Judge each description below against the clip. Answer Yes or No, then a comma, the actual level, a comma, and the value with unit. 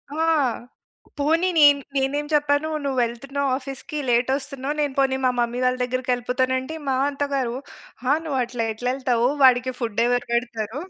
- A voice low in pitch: No, very high, 260 Hz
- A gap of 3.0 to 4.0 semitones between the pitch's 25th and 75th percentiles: No, narrow, 2.4 semitones